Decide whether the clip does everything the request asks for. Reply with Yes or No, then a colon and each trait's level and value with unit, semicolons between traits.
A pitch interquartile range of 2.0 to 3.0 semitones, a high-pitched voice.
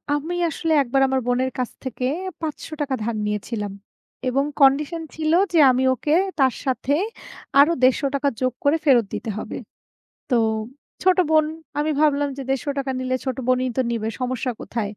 Yes: average, 2.7 semitones; very high, 270 Hz